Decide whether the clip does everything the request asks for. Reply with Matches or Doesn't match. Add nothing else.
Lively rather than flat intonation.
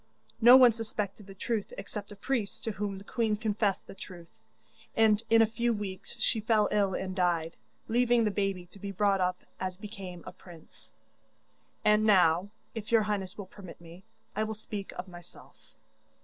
Doesn't match